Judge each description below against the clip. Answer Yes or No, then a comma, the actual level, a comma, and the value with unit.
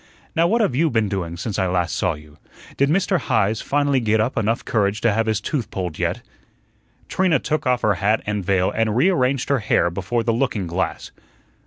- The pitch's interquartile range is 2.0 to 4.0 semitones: No, wide, 5.6 semitones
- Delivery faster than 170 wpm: Yes, fast, 205 wpm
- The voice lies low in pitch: Yes, low, 110 Hz